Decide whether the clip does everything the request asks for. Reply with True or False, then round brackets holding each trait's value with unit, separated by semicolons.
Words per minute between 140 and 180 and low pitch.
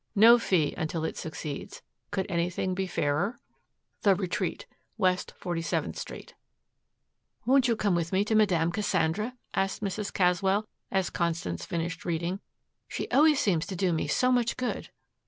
False (150 wpm; 185 Hz)